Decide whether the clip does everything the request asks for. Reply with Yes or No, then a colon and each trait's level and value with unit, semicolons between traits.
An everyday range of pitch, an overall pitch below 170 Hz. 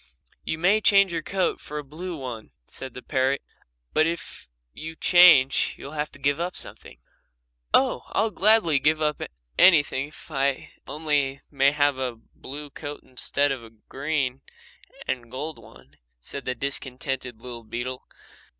Yes: average, 3.4 semitones; medium, 140 Hz